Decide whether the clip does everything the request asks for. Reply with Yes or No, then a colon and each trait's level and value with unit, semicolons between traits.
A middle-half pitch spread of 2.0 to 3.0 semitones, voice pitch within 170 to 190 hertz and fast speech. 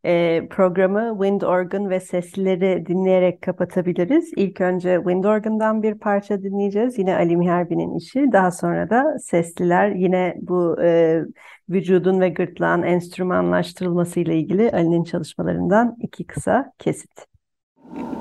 No: narrow, 2.4 semitones; medium, 185 Hz; average, 115 wpm